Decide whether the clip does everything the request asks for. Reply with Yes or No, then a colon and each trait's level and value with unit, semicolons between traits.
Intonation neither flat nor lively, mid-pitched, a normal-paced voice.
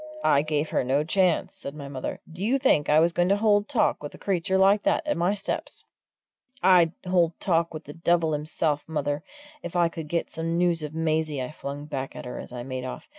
No: average, 3.3 semitones; medium, 165 Hz; fast, 230 wpm